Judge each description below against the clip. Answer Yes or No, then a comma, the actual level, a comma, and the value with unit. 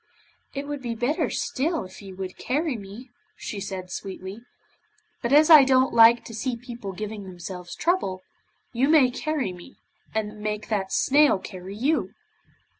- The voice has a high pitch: Yes, high, 225 Hz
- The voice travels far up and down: Yes, wide, 5.8 semitones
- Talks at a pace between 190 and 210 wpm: No, average, 160 wpm